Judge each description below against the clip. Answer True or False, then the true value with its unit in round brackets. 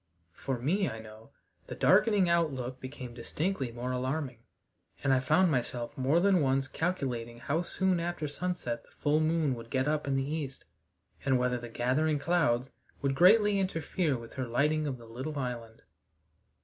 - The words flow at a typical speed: True (170 wpm)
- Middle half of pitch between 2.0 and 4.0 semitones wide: False (4.7 semitones)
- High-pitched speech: False (135 Hz)